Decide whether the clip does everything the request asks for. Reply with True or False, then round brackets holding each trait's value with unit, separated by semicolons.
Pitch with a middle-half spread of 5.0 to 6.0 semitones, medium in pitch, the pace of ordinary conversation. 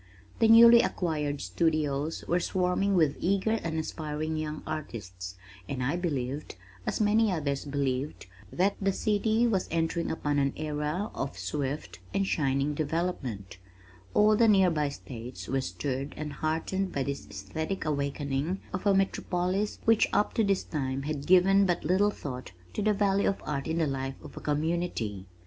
True (5.5 semitones; 155 Hz; 165 wpm)